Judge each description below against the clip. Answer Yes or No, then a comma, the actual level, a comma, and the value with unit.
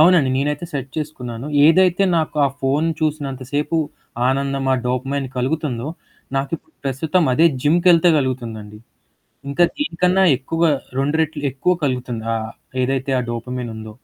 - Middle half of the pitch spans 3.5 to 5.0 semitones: Yes, average, 3.8 semitones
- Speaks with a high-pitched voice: No, medium, 140 Hz